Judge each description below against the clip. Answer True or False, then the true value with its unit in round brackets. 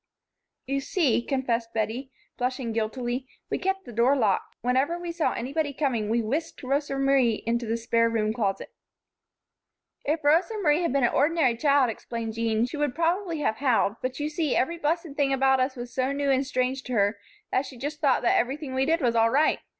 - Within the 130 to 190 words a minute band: False (200 wpm)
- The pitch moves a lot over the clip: False (3.9 semitones)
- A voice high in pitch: True (265 Hz)